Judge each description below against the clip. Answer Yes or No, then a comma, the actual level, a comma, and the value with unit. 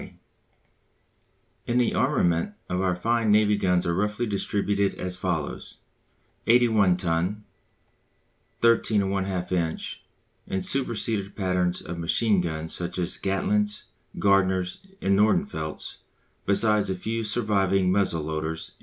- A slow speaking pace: Yes, slow, 120 wpm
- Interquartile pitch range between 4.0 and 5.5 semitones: No, average, 2.8 semitones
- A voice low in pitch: Yes, very low, 95 Hz